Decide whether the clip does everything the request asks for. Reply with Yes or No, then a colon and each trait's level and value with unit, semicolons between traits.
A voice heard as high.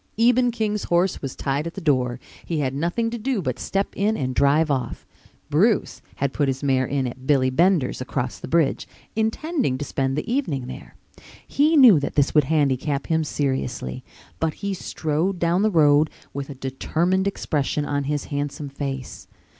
No: medium, 150 Hz